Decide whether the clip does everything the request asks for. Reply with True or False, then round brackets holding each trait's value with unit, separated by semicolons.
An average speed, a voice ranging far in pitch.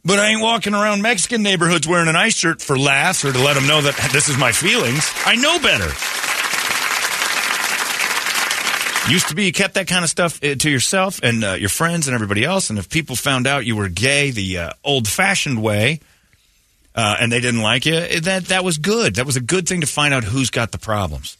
False (220 wpm; 7.0 semitones)